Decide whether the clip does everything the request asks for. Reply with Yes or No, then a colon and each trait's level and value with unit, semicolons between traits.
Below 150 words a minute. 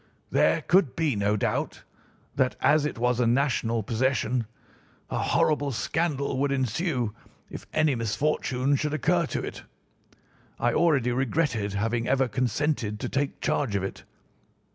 Yes: average, 140 wpm